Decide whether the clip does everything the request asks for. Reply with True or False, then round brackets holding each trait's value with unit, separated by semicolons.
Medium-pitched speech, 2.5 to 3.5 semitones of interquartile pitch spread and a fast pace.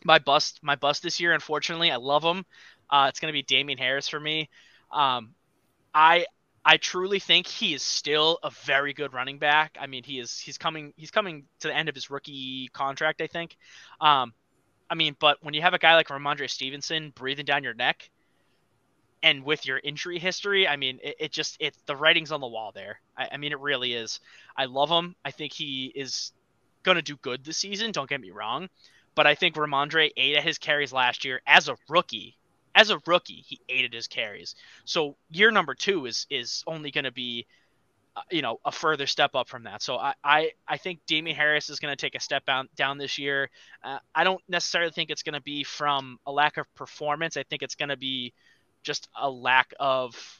True (150 Hz; 2.8 semitones; 220 wpm)